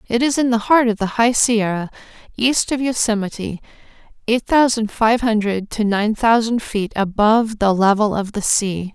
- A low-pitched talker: No, high, 220 Hz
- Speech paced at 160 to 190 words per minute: Yes, average, 175 wpm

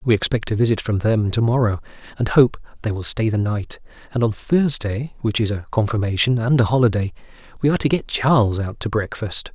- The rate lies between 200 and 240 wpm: Yes, fast, 205 wpm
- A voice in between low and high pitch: No, low, 115 Hz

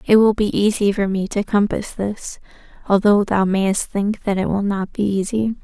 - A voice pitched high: Yes, high, 200 Hz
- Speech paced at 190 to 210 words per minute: Yes, average, 200 wpm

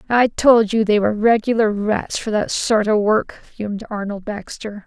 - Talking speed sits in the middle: Yes, average, 185 wpm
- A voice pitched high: Yes, high, 215 Hz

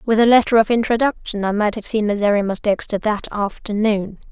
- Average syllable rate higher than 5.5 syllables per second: Yes, 5.7 syllables/s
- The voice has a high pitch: Yes, high, 215 Hz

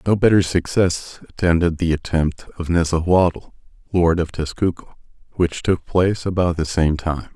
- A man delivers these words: Yes, male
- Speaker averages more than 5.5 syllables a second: No, 4.6 syllables/s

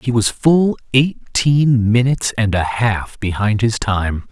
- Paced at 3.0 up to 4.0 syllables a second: Yes, 3.7 syllables/s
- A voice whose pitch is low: Yes, low, 115 Hz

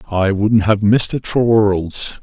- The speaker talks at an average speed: Yes, average, 190 wpm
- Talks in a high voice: No, low, 105 Hz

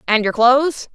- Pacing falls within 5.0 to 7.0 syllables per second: Yes, 5.2 syllables/s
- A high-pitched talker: Yes, very high, 250 Hz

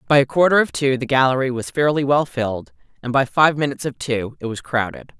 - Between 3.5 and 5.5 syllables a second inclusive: No, 6.0 syllables/s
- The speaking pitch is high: No, low, 135 Hz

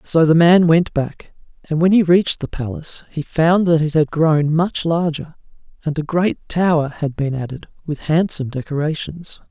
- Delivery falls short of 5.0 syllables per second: Yes, 4.8 syllables/s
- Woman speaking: No, male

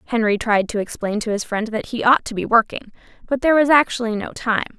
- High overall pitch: Yes, high, 225 Hz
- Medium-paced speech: No, fast, 240 wpm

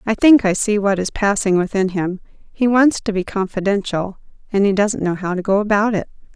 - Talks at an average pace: No, fast, 225 wpm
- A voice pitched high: Yes, high, 200 Hz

